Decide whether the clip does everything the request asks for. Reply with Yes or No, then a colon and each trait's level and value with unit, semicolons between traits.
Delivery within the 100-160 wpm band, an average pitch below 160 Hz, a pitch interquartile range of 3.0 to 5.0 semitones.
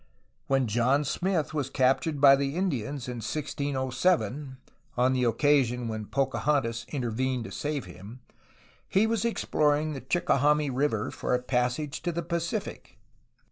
Yes: average, 140 wpm; low, 135 Hz; average, 3.4 semitones